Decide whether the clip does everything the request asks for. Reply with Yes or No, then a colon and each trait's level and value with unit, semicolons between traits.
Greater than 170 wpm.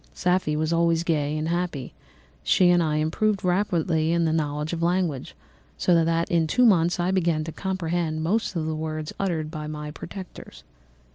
Yes: average, 180 wpm